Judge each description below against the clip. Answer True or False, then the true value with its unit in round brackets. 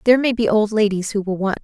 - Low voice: False (215 Hz)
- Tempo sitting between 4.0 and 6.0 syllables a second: False (6.9 syllables/s)